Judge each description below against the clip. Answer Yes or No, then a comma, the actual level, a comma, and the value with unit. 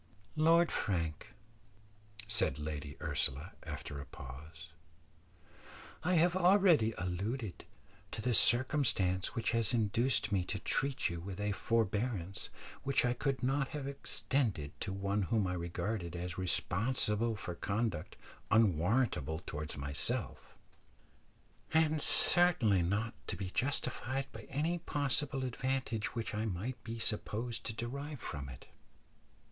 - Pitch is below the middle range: Yes, low, 110 Hz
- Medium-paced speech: No, slow, 125 wpm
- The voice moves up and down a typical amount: No, wide, 6.6 semitones